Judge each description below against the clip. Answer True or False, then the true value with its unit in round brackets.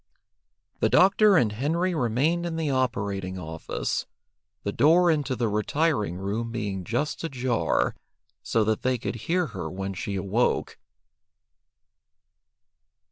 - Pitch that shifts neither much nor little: False (7.5 semitones)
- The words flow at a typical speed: False (125 wpm)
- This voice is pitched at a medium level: False (120 Hz)